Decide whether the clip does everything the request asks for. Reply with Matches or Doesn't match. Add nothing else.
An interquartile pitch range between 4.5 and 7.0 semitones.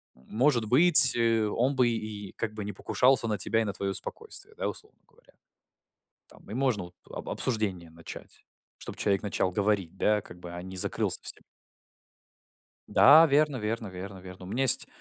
Matches